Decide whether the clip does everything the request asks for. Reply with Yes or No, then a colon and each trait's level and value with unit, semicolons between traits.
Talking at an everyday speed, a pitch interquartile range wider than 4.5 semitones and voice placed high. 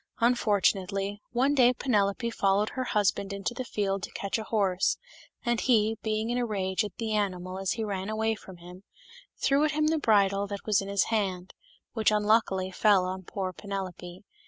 No: average, 185 wpm; narrow, 2.6 semitones; high, 205 Hz